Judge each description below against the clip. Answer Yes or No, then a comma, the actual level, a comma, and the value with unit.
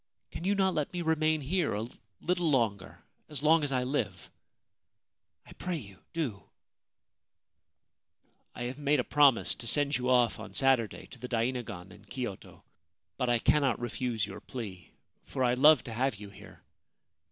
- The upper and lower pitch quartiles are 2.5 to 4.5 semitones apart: No, average, 4.9 semitones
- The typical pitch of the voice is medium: No, low, 125 Hz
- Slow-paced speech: No, average, 175 wpm